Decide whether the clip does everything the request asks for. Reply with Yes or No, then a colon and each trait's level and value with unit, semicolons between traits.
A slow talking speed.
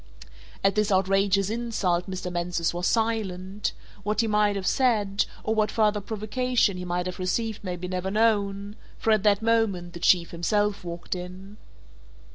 No: average, 165 wpm